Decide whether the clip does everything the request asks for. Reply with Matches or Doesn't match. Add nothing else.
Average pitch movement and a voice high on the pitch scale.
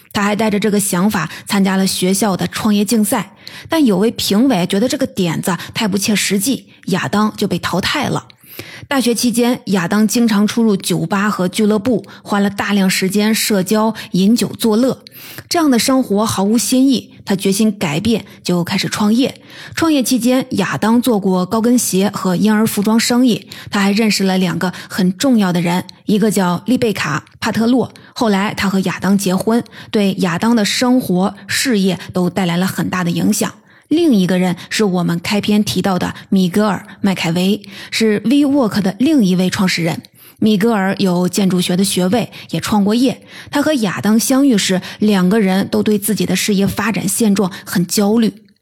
Matches